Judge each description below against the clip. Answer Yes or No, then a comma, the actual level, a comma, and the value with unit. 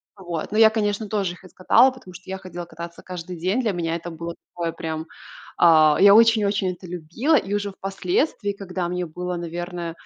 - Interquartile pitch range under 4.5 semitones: Yes, average, 3.0 semitones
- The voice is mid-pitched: Yes, medium, 180 Hz